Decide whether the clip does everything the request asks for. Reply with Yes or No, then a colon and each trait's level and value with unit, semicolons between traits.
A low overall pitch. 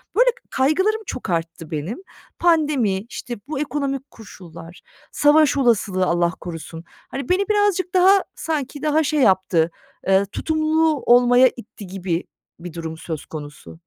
No: high, 245 Hz